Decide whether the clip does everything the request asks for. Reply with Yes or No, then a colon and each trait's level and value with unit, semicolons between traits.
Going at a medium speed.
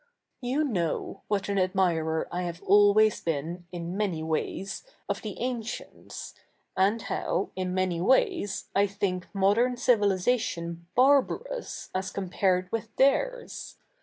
No: slow, 130 wpm